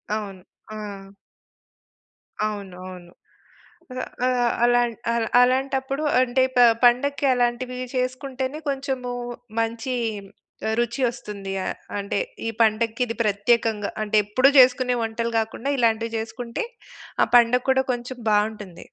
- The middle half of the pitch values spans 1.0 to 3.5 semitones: Yes, average, 2.7 semitones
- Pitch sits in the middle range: No, high, 240 Hz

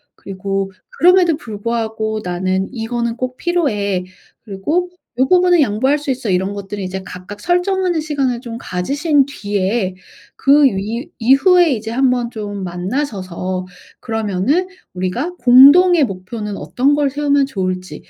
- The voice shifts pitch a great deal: Yes, wide, 6.7 semitones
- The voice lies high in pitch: Yes, high, 235 Hz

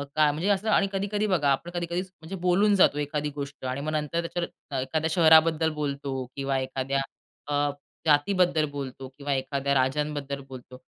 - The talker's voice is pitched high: No, medium, 150 Hz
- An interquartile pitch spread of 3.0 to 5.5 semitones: Yes, average, 3.7 semitones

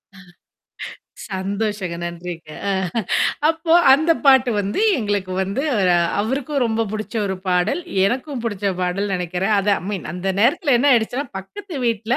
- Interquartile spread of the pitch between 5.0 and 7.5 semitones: Yes, wide, 5.5 semitones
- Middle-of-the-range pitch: No, high, 210 Hz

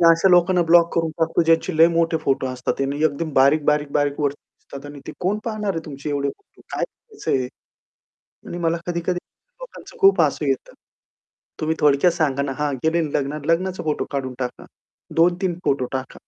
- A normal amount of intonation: Yes, average, 3.6 semitones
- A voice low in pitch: No, medium, 160 Hz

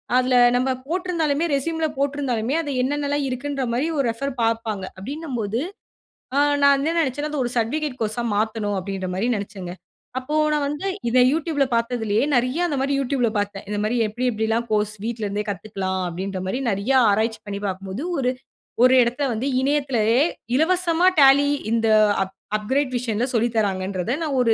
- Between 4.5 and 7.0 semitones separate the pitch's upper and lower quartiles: Yes, average, 5.0 semitones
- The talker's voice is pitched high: Yes, high, 245 Hz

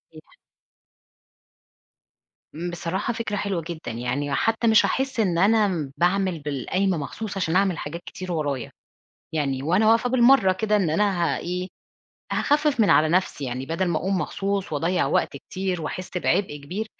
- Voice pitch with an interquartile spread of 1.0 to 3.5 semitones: No, average, 4.7 semitones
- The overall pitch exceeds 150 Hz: Yes, medium, 185 Hz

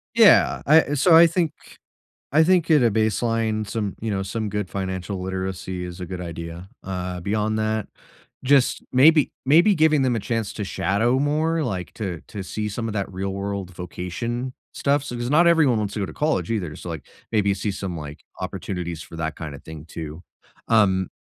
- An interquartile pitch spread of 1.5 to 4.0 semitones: No, wide, 5.6 semitones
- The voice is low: Yes, low, 105 Hz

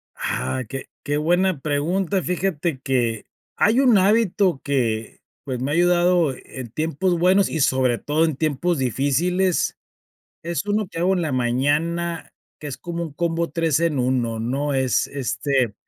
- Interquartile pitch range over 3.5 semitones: Yes, average, 5.0 semitones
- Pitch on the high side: No, medium, 155 Hz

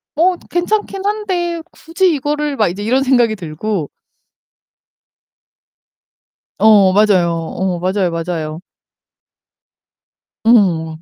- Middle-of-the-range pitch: No, high, 215 Hz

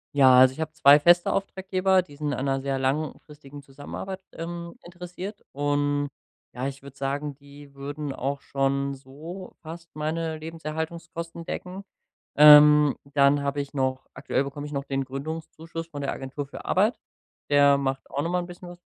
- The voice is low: No, medium, 145 Hz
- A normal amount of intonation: Yes, average, 3.1 semitones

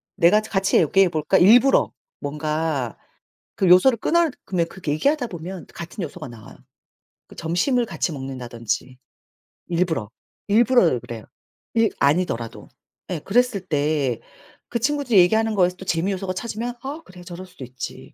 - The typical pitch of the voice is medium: Yes, medium, 180 Hz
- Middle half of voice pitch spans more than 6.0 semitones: Yes, wide, 6.4 semitones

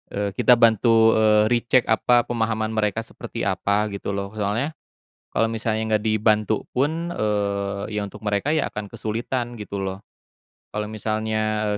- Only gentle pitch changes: Yes, narrow, 1.8 semitones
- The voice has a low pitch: Yes, low, 110 Hz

